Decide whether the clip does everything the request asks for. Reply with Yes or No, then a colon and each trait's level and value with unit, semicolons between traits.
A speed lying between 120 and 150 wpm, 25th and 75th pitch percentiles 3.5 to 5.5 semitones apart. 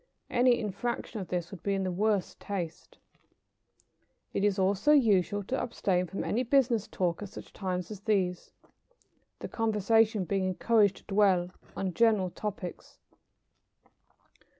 No: average, 140 wpm; average, 3.1 semitones